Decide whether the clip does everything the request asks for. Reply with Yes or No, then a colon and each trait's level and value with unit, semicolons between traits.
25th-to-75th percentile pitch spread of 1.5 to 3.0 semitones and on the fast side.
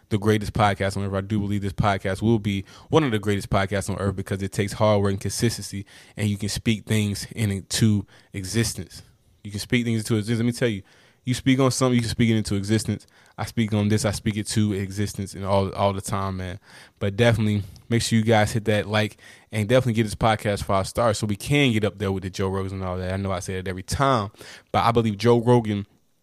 Yes: narrow, 2.6 semitones; fast, 250 wpm